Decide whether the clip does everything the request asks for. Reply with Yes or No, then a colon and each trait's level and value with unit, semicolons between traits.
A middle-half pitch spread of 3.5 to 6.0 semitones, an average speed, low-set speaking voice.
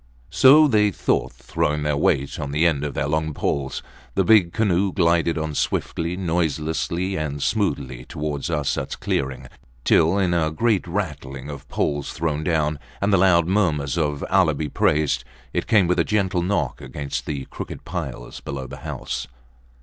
Yes: average, 4.1 semitones; average, 165 wpm; very low, 80 Hz